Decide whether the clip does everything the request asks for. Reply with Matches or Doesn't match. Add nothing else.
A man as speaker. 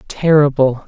Matches